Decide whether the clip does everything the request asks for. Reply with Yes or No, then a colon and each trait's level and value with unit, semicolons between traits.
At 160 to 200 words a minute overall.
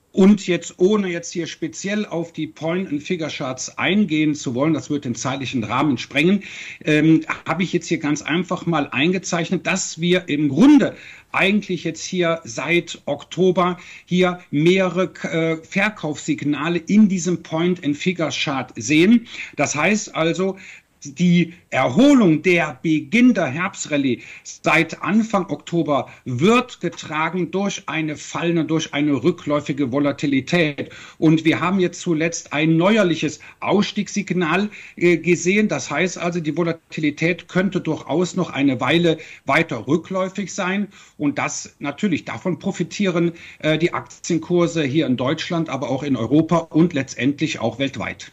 No: average, 130 wpm